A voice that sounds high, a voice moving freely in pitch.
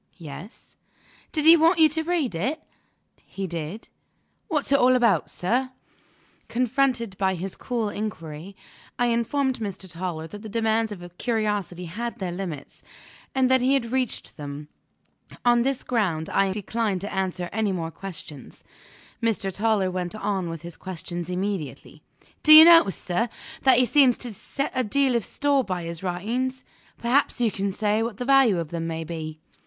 Yes: high, 210 Hz; wide, 5.9 semitones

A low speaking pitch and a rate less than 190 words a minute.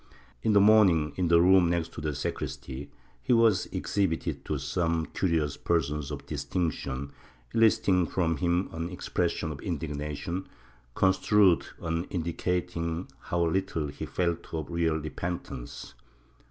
Yes: very low, 85 Hz; slow, 135 wpm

